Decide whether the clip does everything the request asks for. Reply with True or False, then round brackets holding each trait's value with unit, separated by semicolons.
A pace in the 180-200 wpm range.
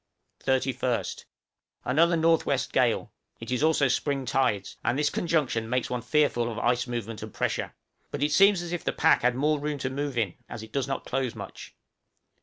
True (190 wpm)